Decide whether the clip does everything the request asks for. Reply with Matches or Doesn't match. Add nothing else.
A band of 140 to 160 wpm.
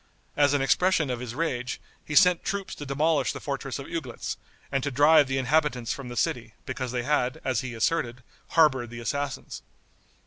Doesn't match